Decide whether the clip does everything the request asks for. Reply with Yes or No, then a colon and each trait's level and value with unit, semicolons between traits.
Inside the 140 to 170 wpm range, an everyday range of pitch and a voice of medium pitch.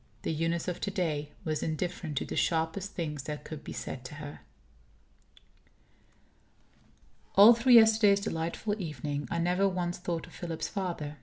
Yes: average, 155 wpm; average, 4.0 semitones; medium, 170 Hz